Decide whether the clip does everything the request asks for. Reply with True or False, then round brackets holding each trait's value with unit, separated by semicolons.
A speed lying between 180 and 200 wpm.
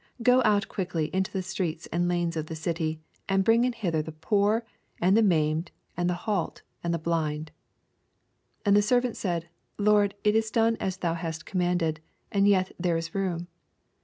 True (190 wpm)